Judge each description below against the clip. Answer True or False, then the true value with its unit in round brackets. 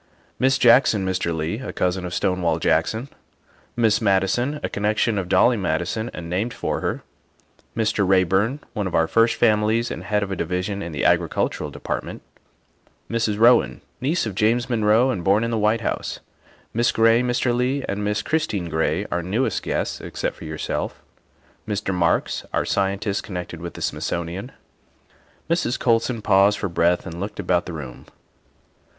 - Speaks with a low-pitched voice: True (105 Hz)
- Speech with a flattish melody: False (4.3 semitones)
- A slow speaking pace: False (170 wpm)